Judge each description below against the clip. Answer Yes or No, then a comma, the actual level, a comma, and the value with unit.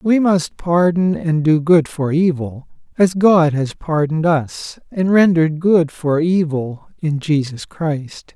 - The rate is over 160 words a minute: No, average, 150 wpm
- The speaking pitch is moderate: Yes, medium, 165 Hz